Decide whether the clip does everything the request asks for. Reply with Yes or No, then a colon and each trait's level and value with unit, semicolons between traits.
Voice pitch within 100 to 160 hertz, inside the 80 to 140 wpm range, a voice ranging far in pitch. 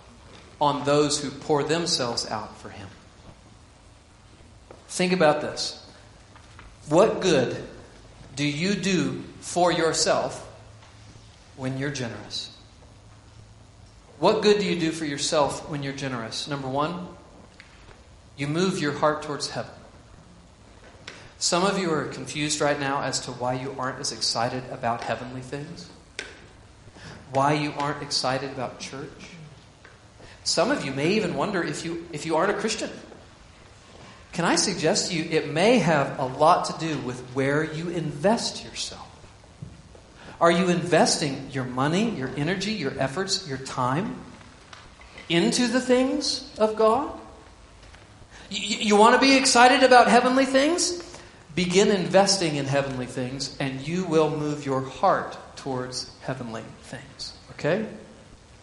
Yes: medium, 140 Hz; slow, 135 wpm; wide, 7.1 semitones